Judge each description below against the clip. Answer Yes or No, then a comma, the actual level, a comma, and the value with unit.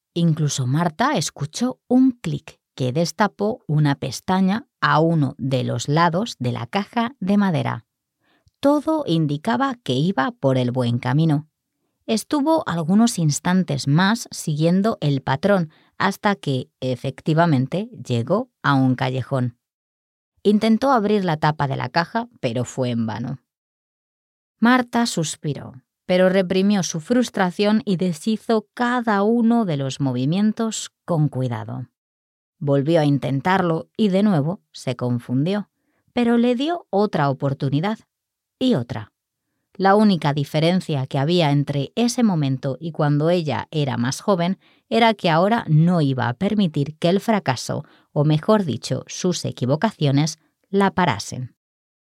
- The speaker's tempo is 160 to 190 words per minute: No, average, 130 wpm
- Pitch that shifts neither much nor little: No, wide, 7.0 semitones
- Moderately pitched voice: Yes, medium, 165 Hz